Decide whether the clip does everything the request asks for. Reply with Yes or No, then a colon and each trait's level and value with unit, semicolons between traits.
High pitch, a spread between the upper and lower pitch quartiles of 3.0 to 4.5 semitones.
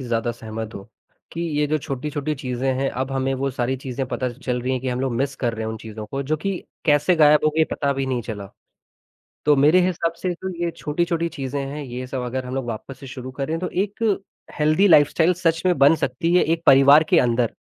No: low, 135 Hz; average, 3.6 semitones